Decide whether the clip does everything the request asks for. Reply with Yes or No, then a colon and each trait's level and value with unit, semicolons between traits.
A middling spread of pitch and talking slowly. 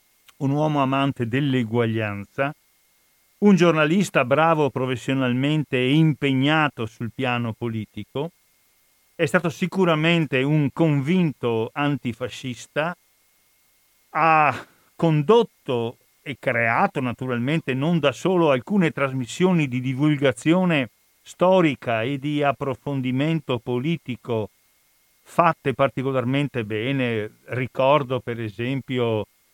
Yes: average, 4.2 semitones; slow, 85 wpm